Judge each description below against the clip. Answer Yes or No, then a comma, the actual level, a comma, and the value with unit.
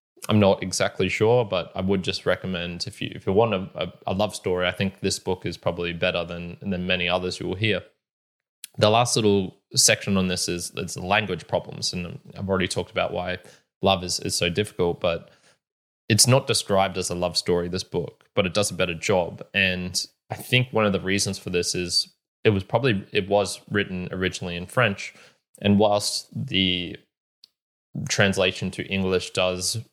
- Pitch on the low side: Yes, very low, 95 Hz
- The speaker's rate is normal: Yes, average, 190 wpm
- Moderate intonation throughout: No, narrow, 2.3 semitones